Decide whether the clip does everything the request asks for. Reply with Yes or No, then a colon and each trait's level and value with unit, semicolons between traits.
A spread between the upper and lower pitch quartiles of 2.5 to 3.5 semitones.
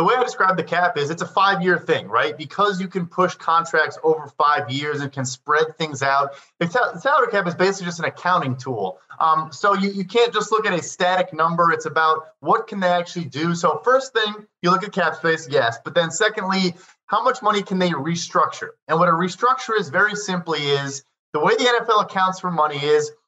No: average, 4.1 semitones